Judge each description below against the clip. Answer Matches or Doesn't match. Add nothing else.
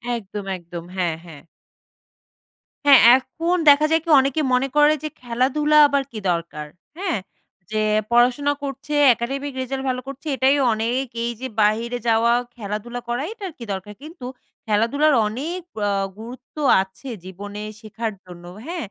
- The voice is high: Matches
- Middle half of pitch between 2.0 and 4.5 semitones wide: Doesn't match